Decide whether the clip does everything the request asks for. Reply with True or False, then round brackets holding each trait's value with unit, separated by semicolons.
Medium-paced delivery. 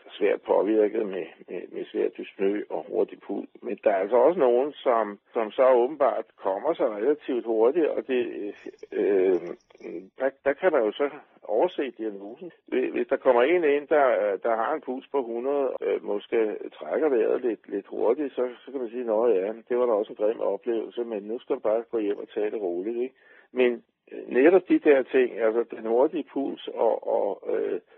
True (200 wpm)